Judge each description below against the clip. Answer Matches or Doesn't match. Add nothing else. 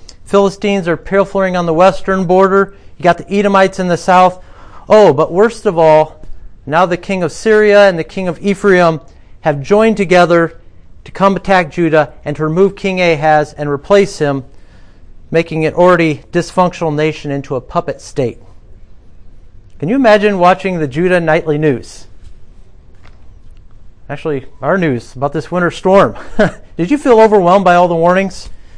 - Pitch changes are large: Matches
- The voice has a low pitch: Doesn't match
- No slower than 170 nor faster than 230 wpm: Doesn't match